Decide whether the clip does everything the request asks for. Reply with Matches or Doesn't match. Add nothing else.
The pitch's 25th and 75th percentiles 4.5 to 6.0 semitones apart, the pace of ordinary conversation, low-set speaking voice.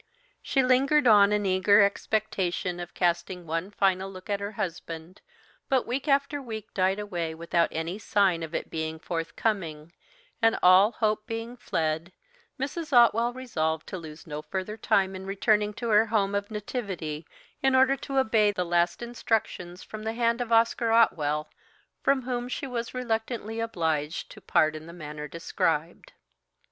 Doesn't match